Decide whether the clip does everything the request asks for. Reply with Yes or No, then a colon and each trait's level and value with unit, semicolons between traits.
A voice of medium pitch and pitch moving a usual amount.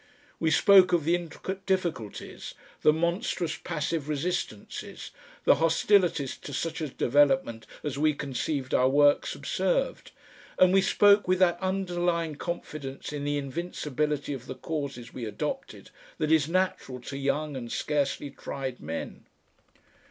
Yes: medium, 155 Hz; average, 4.0 semitones